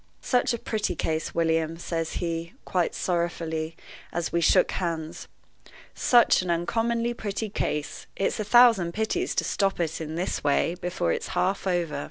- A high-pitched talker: No, medium, 175 Hz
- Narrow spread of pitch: No, average, 3.8 semitones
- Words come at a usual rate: Yes, average, 160 wpm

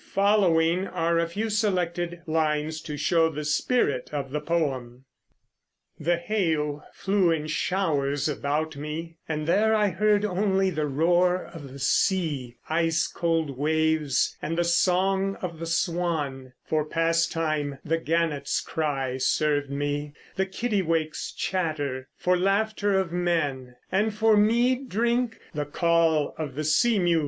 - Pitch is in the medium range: Yes, medium, 165 Hz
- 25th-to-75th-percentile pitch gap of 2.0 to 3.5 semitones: No, average, 4.0 semitones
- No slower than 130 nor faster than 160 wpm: Yes, average, 140 wpm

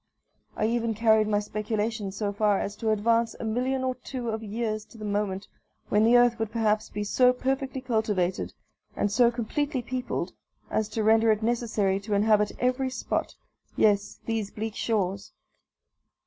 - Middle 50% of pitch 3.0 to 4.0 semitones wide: No, narrow, 2.4 semitones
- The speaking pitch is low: No, high, 220 Hz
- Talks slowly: No, average, 165 wpm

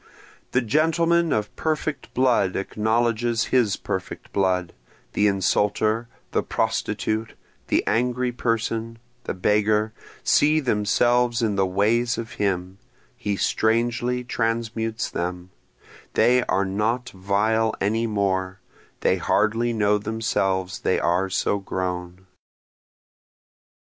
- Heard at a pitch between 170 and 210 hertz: No, low, 110 Hz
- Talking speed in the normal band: No, slow, 110 wpm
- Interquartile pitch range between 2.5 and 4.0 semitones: Yes, average, 3.4 semitones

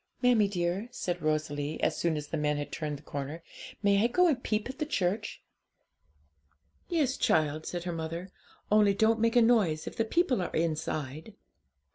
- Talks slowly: No, average, 180 wpm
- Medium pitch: Yes, medium, 180 Hz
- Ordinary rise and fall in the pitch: No, wide, 6.6 semitones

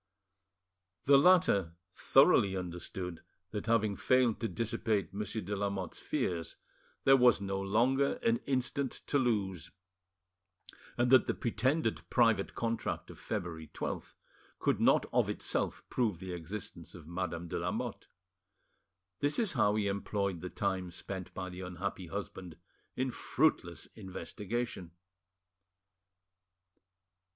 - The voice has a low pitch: Yes, low, 100 Hz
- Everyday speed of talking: No, slow, 125 wpm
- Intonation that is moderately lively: Yes, average, 4.7 semitones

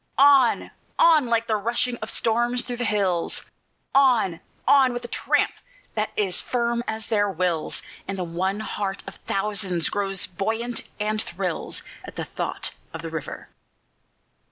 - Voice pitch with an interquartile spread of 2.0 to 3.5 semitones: No, average, 4.0 semitones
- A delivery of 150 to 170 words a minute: Yes, average, 155 wpm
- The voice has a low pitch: No, high, 215 Hz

